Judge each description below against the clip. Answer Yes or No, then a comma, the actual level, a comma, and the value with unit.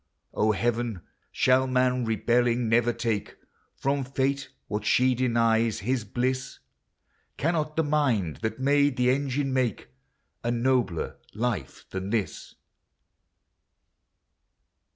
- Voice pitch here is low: Yes, low, 125 Hz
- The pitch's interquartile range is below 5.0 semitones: Yes, average, 2.7 semitones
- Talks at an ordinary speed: No, slow, 110 wpm